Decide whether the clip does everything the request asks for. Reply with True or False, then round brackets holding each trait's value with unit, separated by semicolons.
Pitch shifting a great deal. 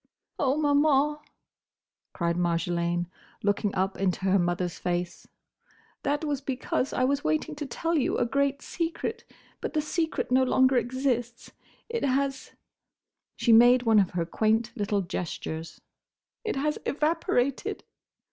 True (7.1 semitones)